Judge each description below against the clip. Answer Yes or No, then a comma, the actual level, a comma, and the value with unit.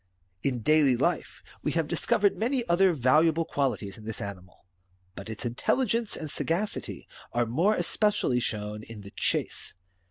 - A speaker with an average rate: Yes, average, 155 wpm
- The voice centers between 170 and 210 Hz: No, medium, 140 Hz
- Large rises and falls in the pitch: Yes, wide, 8.3 semitones